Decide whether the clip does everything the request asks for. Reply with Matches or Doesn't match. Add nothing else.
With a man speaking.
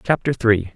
Matches